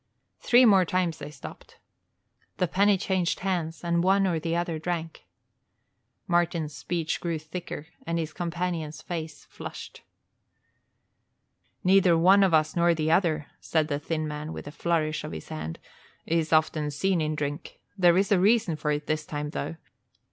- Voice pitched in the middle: Yes, medium, 165 Hz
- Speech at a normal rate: Yes, average, 160 wpm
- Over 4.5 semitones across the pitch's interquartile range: No, narrow, 2.5 semitones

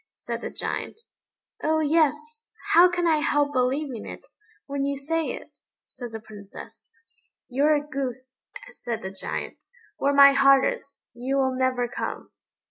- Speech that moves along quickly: No, average, 150 wpm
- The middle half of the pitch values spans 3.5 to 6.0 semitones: No, average, 2.8 semitones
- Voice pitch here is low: No, very high, 275 Hz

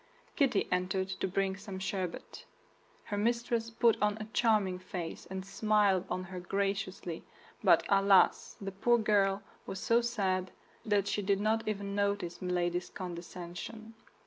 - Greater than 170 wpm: No, average, 145 wpm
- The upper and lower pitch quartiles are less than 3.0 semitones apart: Yes, narrow, 2.5 semitones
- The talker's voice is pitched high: Yes, high, 195 Hz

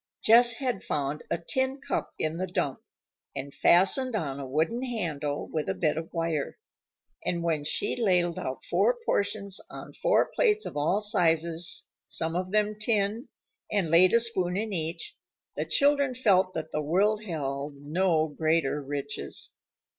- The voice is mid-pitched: Yes, medium, 175 Hz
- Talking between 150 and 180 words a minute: Yes, average, 160 wpm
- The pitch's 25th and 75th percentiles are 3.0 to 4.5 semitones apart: No, wide, 5.5 semitones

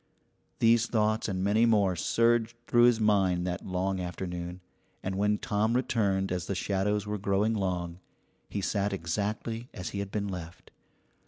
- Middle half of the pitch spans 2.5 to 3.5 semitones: Yes, average, 2.8 semitones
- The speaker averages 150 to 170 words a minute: Yes, average, 160 wpm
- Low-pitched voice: Yes, low, 100 Hz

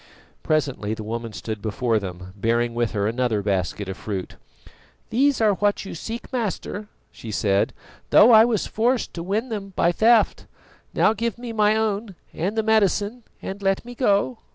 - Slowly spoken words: No, average, 175 wpm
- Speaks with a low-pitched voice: No, high, 195 Hz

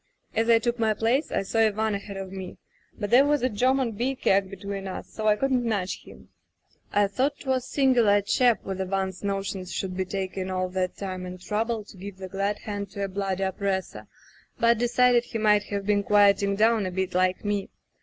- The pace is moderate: No, fast, 210 wpm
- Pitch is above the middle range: Yes, high, 200 Hz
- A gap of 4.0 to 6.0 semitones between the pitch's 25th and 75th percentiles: No, average, 3.1 semitones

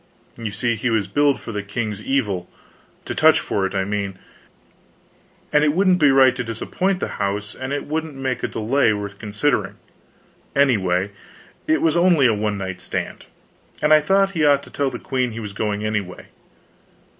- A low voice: Yes, low, 115 Hz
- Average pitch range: No, wide, 5.9 semitones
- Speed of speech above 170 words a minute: Yes, average, 185 wpm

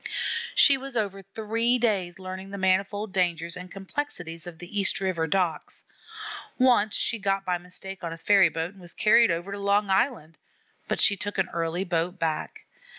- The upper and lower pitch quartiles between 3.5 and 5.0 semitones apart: No, average, 2.7 semitones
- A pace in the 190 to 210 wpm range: No, average, 175 wpm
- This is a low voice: No, high, 190 Hz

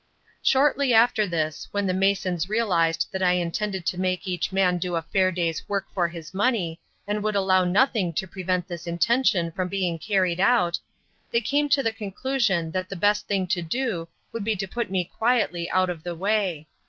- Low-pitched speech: No, medium, 185 Hz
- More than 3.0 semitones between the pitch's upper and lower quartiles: Yes, average, 3.4 semitones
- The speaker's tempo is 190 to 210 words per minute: Yes, average, 195 wpm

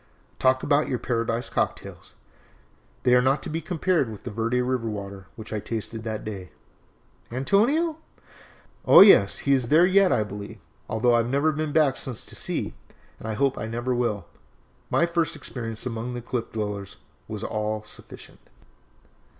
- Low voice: Yes, low, 120 Hz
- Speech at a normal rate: Yes, average, 170 wpm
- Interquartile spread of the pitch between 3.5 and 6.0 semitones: Yes, average, 4.5 semitones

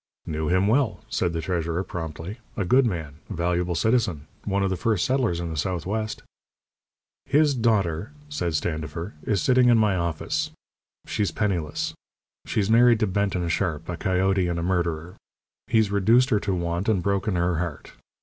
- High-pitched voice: No, very low, 95 Hz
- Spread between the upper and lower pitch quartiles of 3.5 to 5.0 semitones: Yes, average, 4.2 semitones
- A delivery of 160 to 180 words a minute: Yes, average, 170 wpm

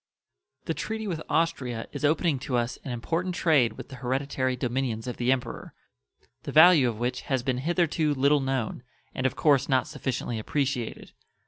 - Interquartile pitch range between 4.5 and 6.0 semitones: No, average, 3.5 semitones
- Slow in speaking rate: No, average, 175 wpm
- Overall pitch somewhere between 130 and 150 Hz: Yes, low, 135 Hz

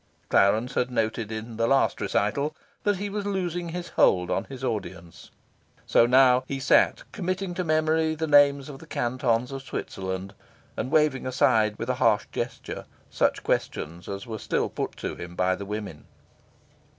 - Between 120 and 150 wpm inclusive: No, average, 170 wpm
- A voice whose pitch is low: Yes, low, 125 Hz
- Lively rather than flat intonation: Yes, wide, 6.8 semitones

